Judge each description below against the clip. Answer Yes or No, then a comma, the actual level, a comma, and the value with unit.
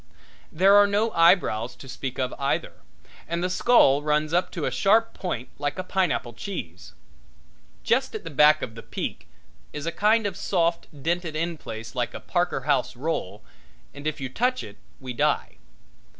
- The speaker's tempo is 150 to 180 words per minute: Yes, average, 170 wpm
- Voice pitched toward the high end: No, medium, 160 Hz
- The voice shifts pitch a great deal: Yes, wide, 5.9 semitones